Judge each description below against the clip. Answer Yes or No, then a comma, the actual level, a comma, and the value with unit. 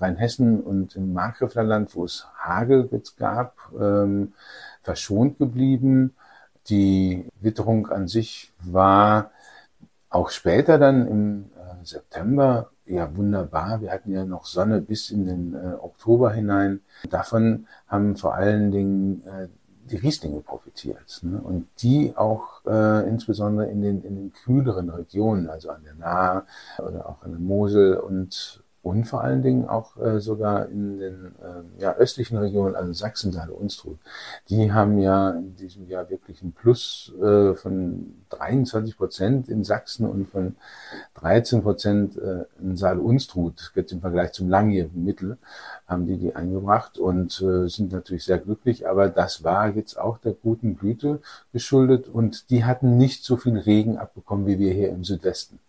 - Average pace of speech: Yes, average, 155 wpm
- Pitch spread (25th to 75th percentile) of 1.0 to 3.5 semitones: Yes, average, 3.2 semitones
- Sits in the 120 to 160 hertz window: No, low, 100 Hz